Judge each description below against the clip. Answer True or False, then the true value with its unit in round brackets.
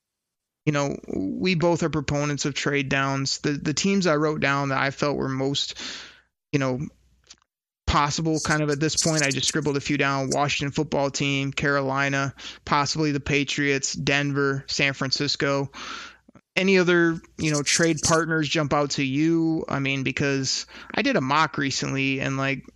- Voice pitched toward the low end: False (145 Hz)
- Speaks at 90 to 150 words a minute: False (170 wpm)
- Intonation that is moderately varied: False (2.0 semitones)